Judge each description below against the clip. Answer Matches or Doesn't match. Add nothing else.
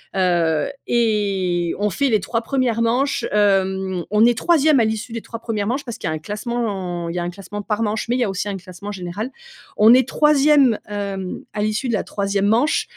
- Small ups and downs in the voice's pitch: Doesn't match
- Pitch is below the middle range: Doesn't match